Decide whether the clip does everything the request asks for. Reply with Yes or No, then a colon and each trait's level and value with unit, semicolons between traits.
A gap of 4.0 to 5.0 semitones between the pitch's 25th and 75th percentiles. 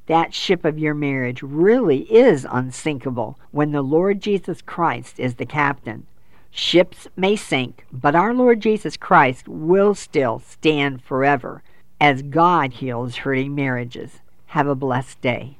Yes: average, 4.5 semitones